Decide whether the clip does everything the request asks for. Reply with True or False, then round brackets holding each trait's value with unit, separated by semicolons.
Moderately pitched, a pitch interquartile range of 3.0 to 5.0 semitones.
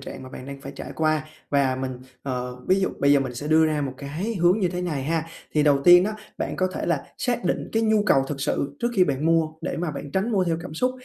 True (155 Hz; 4.5 semitones)